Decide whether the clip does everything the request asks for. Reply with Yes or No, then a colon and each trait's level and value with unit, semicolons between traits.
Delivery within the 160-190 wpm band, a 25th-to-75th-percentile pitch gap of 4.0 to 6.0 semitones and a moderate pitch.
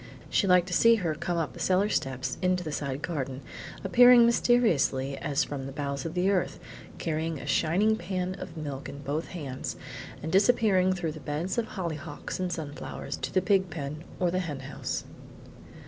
Yes: average, 185 wpm; average, 4.4 semitones; medium, 170 Hz